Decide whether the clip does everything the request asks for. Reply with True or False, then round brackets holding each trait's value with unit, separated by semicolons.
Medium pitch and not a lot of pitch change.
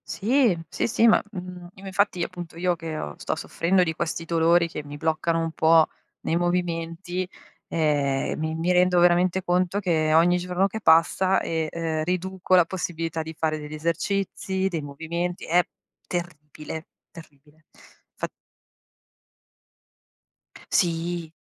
True (170 Hz; 2.1 semitones)